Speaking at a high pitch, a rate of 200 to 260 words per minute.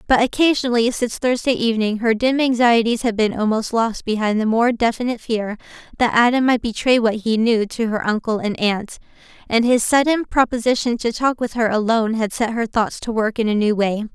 Yes: high, 230 Hz; fast, 205 wpm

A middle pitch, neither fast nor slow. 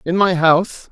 Yes: medium, 175 Hz; average, 195 wpm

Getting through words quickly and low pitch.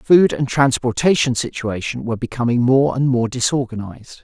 No: average, 155 wpm; low, 125 Hz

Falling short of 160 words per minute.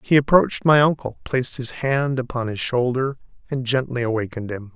No: average, 175 wpm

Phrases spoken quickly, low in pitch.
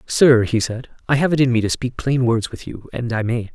Yes: fast, 290 wpm; low, 120 Hz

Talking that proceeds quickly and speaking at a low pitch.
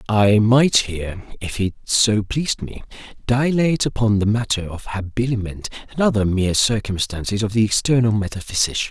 No: slow, 135 wpm; low, 110 Hz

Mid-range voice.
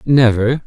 No: low, 125 Hz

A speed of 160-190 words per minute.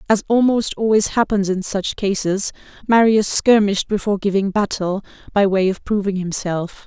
No: average, 150 wpm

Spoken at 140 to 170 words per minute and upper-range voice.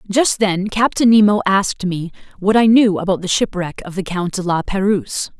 No: average, 200 wpm; high, 195 Hz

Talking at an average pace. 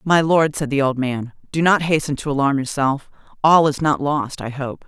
No: fast, 220 wpm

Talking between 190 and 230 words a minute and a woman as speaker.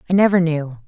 Yes: fast, 205 wpm; female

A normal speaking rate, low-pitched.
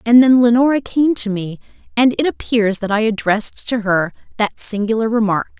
No: average, 180 wpm; high, 225 Hz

